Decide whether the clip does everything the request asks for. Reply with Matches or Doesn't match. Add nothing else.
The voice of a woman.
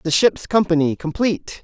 Doesn't match